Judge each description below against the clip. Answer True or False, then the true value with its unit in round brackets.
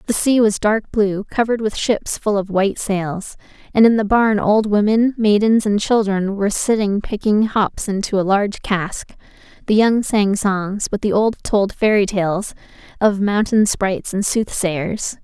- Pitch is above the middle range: True (205 Hz)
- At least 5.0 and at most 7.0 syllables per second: False (4.4 syllables/s)